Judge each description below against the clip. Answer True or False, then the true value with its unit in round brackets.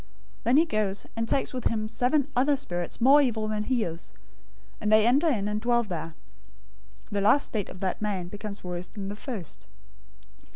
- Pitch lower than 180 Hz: False (215 Hz)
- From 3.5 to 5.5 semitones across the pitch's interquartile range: True (4.2 semitones)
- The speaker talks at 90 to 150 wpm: False (195 wpm)